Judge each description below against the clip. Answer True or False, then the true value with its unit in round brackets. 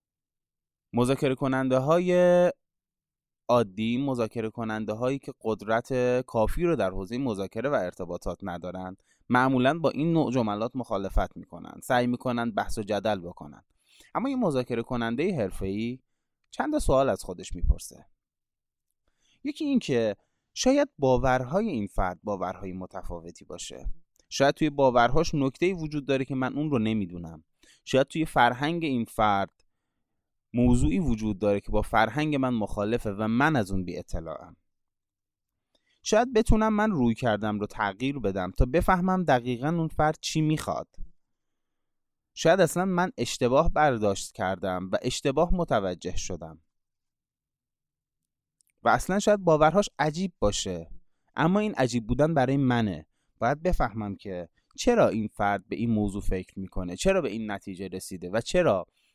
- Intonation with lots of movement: True (6.9 semitones)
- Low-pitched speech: True (120 Hz)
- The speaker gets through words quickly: False (140 wpm)